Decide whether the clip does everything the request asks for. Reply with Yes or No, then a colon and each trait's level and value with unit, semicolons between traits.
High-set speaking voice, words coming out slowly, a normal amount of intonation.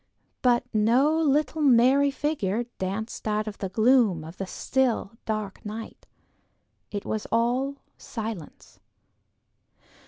Yes: high, 230 Hz; slow, 115 wpm; average, 4.1 semitones